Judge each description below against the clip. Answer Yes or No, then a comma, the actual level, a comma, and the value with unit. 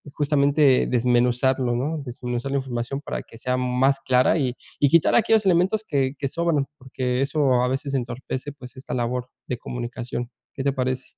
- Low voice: Yes, low, 130 Hz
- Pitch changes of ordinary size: No, narrow, 2.2 semitones